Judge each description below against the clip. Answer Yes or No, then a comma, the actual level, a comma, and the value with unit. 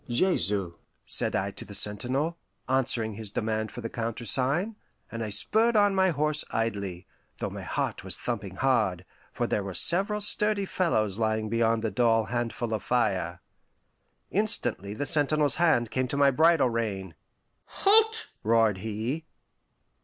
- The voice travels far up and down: Yes, wide, 6.4 semitones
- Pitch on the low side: Yes, low, 120 Hz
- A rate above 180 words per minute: No, average, 150 wpm